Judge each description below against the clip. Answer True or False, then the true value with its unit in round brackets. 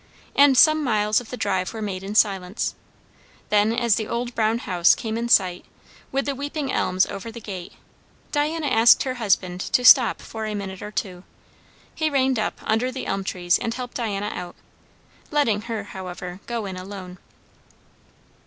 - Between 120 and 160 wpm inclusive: False (175 wpm)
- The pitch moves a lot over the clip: False (4.5 semitones)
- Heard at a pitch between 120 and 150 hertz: False (220 Hz)